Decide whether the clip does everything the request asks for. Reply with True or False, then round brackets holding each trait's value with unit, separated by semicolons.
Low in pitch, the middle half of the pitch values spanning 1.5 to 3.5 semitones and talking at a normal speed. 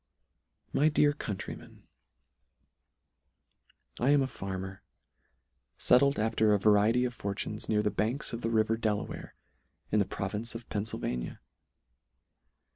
False (110 Hz; 2.9 semitones; 120 wpm)